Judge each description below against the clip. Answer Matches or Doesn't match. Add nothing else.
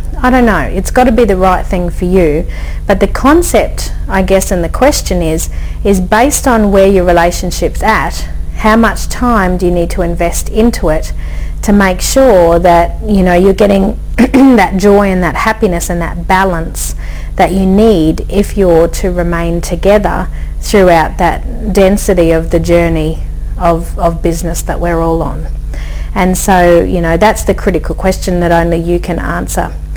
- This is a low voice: Doesn't match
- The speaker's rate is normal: Matches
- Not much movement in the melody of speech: Doesn't match